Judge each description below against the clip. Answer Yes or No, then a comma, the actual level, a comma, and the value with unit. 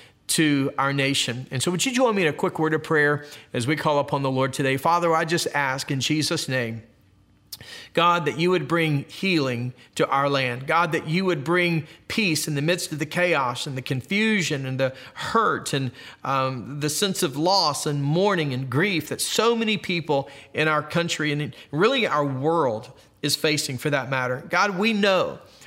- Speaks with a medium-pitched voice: Yes, medium, 150 Hz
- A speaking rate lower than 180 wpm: No, average, 200 wpm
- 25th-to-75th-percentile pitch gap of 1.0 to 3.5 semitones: No, average, 4.2 semitones